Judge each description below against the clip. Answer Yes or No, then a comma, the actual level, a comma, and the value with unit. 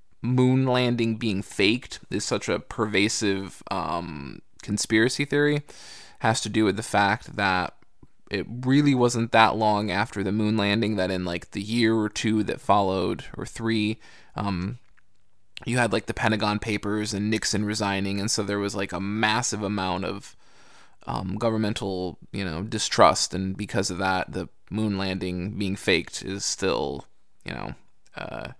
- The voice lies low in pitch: Yes, low, 105 Hz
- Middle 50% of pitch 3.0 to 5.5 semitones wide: No, narrow, 2.4 semitones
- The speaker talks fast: No, average, 160 wpm